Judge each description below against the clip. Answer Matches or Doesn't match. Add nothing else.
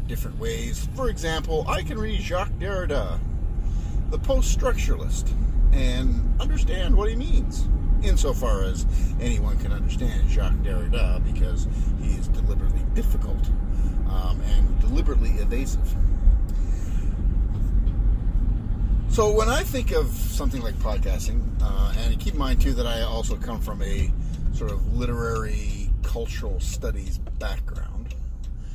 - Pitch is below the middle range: Matches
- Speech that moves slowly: Matches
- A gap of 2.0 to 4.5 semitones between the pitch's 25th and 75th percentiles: Doesn't match